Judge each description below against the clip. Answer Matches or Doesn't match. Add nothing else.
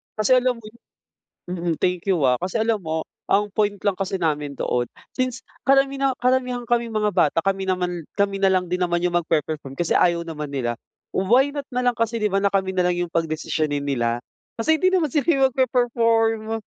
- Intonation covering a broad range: Matches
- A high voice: Matches